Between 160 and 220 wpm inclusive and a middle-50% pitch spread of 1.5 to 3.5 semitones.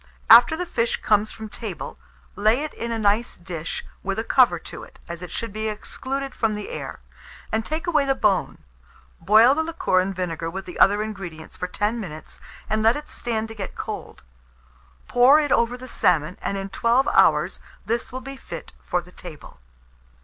No: average, 195 wpm; average, 4.5 semitones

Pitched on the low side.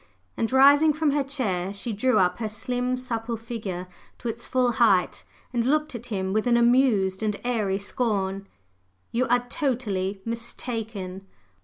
No: high, 230 Hz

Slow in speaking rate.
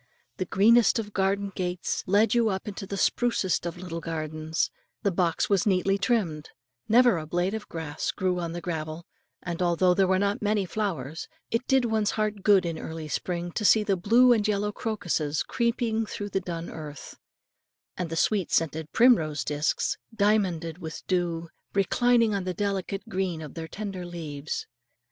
No: average, 170 wpm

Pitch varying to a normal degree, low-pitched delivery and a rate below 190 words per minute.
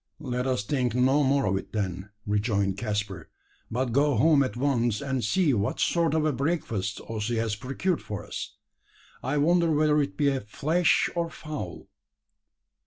No: wide, 5.9 semitones; low, 130 Hz; average, 165 wpm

